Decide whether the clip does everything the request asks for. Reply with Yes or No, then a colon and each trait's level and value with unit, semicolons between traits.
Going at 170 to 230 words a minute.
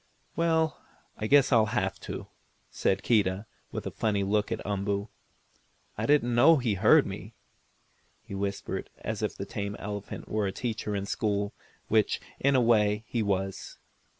No: average, 160 wpm